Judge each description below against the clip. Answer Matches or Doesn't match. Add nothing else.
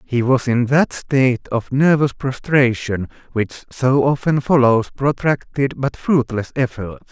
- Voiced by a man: Matches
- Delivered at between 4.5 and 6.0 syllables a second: Doesn't match